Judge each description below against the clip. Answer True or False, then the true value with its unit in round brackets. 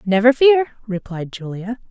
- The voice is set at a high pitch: True (225 Hz)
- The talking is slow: True (125 wpm)